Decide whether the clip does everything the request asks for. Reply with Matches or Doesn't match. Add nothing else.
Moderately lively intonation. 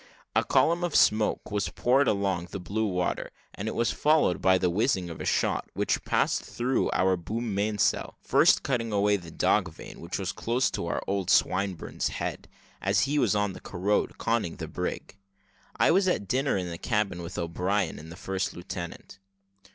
Matches